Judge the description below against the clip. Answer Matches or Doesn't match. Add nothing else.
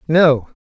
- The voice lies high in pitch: Doesn't match